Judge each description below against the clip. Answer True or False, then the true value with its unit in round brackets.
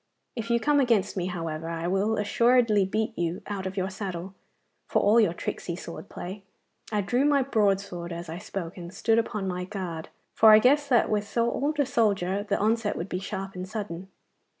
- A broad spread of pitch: False (3.8 semitones)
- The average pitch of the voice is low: False (200 Hz)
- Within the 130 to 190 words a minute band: False (200 wpm)